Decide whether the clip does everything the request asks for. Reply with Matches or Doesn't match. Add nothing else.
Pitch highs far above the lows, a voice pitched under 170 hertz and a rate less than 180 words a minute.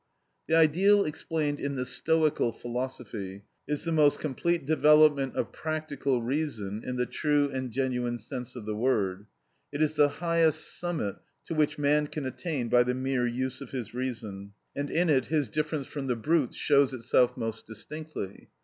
Doesn't match